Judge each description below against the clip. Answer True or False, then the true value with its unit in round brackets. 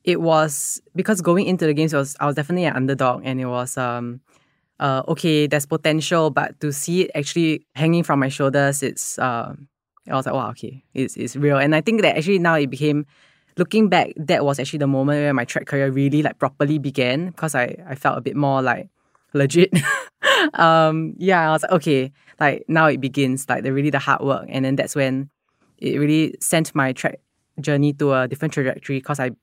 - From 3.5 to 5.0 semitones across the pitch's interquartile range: False (3.0 semitones)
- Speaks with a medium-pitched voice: True (145 Hz)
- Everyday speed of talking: False (215 wpm)